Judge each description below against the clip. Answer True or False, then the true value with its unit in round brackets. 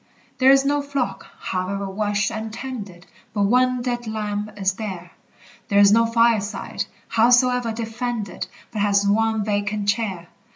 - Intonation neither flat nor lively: True (3.0 semitones)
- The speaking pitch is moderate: False (215 Hz)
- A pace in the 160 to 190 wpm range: False (140 wpm)